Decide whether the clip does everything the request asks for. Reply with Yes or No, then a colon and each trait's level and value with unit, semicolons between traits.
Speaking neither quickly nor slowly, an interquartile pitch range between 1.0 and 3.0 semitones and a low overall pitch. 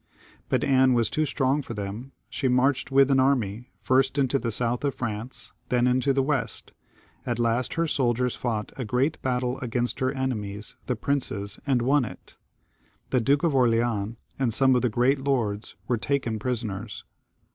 Yes: average, 175 wpm; narrow, 2.5 semitones; low, 125 Hz